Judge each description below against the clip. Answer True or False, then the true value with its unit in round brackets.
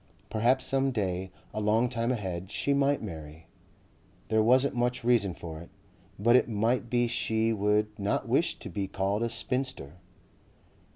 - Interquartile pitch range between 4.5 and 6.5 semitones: False (3.8 semitones)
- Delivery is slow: False (160 wpm)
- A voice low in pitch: True (110 Hz)